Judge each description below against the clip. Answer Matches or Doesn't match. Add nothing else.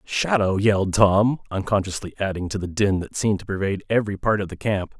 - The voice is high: Doesn't match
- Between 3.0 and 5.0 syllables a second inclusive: Doesn't match